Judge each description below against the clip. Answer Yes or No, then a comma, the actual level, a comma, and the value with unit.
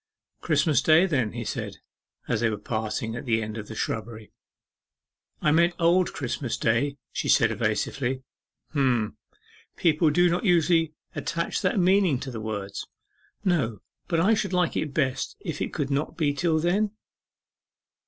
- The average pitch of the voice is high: No, medium, 145 Hz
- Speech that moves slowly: No, average, 160 wpm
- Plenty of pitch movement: Yes, wide, 6.9 semitones